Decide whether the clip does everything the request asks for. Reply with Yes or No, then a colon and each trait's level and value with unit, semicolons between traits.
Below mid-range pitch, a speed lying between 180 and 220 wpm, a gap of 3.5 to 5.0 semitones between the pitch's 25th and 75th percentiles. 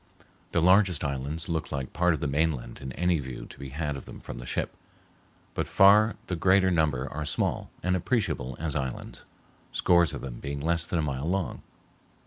Yes: very low, 80 Hz; average, 195 wpm; average, 4.4 semitones